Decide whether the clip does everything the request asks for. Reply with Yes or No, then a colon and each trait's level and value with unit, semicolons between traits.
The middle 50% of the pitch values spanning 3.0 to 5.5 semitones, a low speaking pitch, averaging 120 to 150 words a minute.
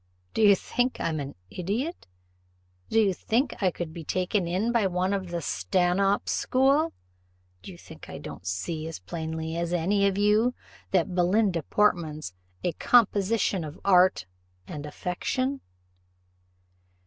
No: average, 4.1 semitones; medium, 185 Hz; average, 145 wpm